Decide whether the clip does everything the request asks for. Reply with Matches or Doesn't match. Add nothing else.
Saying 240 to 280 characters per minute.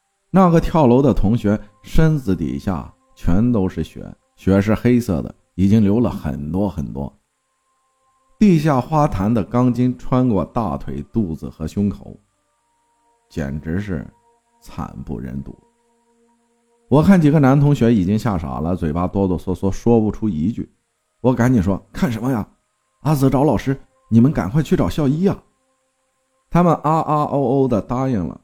Doesn't match